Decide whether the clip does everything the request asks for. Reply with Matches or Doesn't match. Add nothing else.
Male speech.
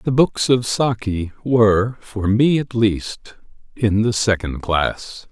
Matches